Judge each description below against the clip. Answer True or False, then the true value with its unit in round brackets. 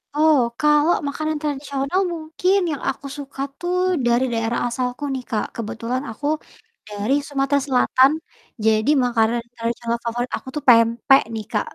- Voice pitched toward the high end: True (260 Hz)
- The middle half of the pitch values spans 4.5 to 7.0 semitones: False (4.0 semitones)